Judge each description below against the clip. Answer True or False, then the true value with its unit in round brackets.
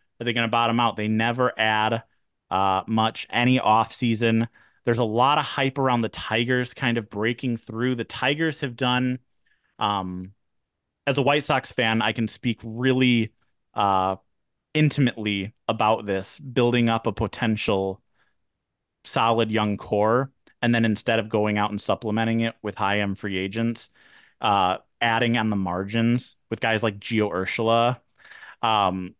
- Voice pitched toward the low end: True (115 Hz)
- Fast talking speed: False (155 wpm)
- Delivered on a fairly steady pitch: True (2.3 semitones)